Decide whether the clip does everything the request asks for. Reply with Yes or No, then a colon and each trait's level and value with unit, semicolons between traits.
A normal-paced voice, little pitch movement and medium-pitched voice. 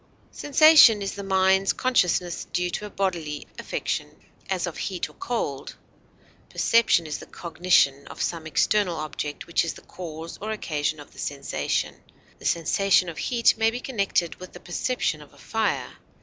No: average, 165 wpm; average, 4.6 semitones; medium, 180 Hz